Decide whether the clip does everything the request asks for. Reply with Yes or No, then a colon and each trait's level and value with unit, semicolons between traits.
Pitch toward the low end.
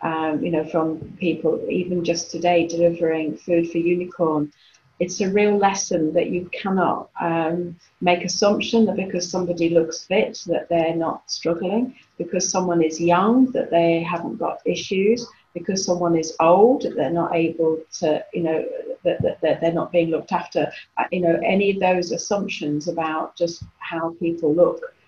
No: medium, 170 Hz